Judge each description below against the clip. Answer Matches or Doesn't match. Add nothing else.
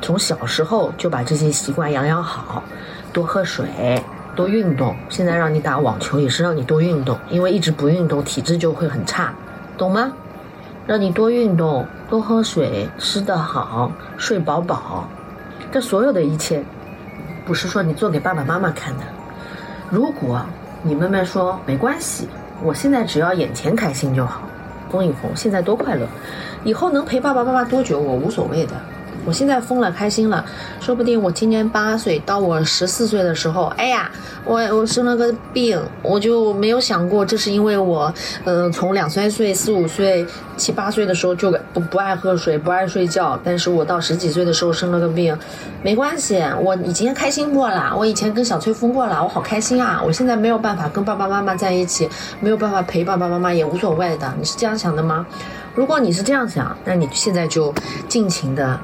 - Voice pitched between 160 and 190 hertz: Matches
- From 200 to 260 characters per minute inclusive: Doesn't match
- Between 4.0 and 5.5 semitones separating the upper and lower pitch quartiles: Matches